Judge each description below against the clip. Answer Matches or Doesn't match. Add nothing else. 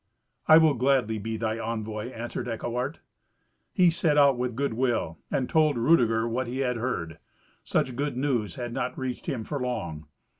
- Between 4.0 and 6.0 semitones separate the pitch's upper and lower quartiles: Doesn't match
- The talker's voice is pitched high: Doesn't match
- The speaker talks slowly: Doesn't match